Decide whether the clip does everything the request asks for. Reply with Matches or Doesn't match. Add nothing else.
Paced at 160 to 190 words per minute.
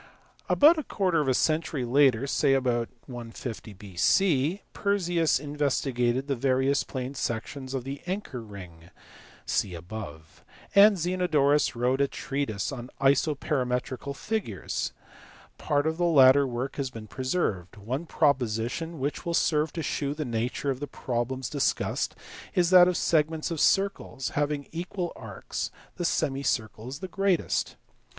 Doesn't match